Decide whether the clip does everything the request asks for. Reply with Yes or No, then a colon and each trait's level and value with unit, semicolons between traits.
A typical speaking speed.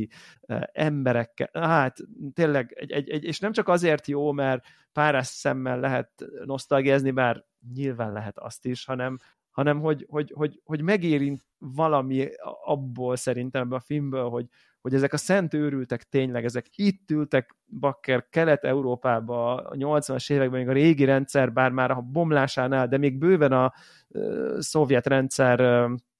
Yes: average, 145 wpm